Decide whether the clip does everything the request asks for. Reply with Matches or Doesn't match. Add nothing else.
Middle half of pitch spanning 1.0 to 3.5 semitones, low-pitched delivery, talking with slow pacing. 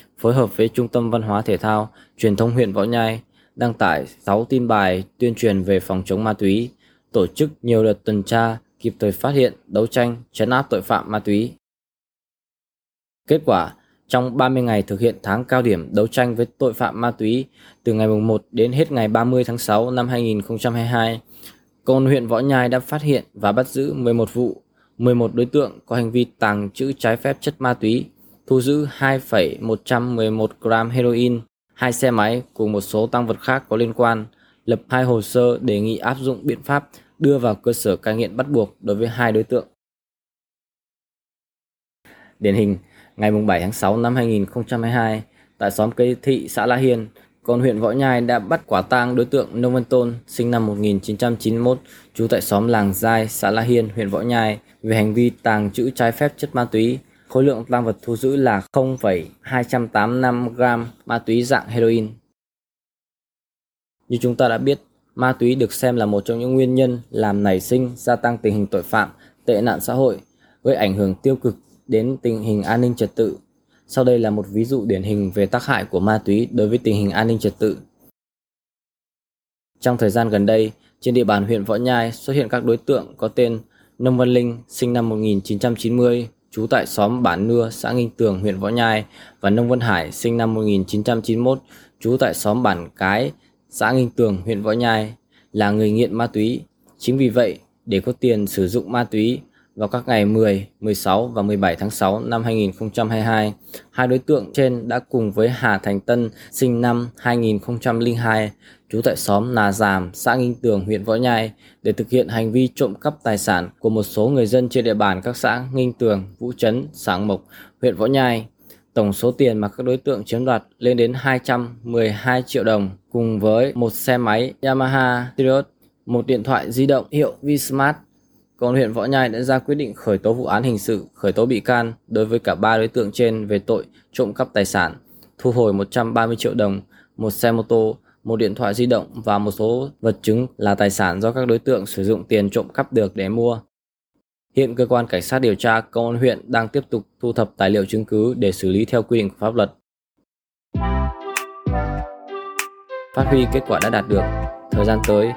Doesn't match